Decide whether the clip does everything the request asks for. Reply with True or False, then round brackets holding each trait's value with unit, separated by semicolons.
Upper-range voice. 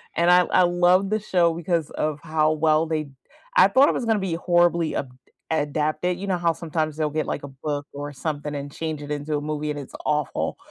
False (155 Hz)